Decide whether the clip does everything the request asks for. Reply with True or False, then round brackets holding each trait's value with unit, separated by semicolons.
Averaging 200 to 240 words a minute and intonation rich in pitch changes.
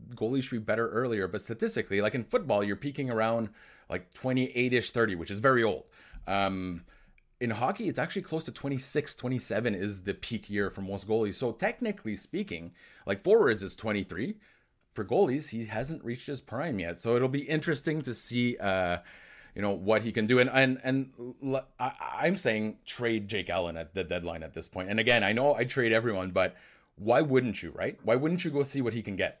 False (205 wpm; 4.9 semitones)